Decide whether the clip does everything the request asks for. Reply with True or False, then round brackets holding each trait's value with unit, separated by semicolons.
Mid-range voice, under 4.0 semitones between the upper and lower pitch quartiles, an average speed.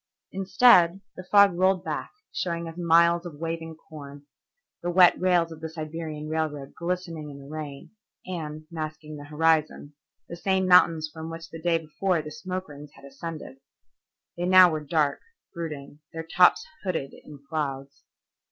True (165 Hz; 2.6 semitones; 160 wpm)